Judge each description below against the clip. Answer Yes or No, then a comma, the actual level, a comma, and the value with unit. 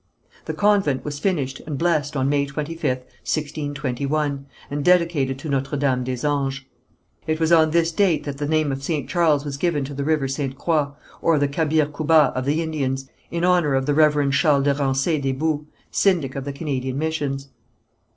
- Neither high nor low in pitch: Yes, medium, 145 Hz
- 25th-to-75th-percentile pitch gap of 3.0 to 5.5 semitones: No, narrow, 2.6 semitones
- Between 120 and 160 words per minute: No, average, 190 wpm